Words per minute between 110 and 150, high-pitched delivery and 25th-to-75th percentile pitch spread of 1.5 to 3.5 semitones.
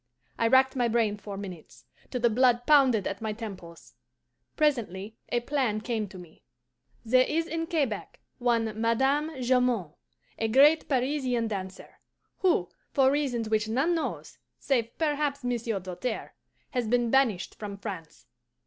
No: average, 145 wpm; high, 240 Hz; average, 4.0 semitones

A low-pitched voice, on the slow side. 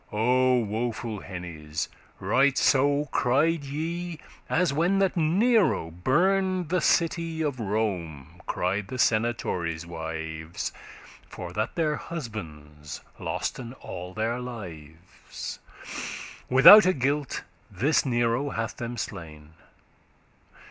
Yes: low, 120 Hz; slow, 100 wpm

